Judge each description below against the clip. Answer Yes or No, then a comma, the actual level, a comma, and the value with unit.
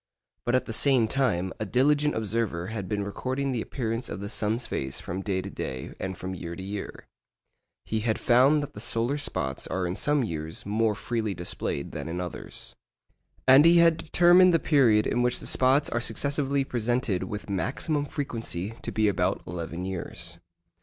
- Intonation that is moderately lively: No, wide, 6.1 semitones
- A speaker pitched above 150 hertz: No, low, 110 Hz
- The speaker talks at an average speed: Yes, average, 185 wpm